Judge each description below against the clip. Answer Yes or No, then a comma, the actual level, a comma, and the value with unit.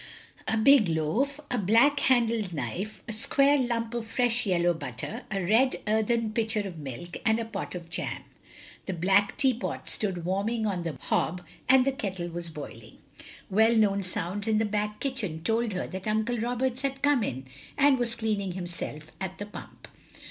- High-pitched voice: Yes, high, 215 Hz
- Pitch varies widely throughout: No, average, 4.9 semitones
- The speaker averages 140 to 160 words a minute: No, average, 175 wpm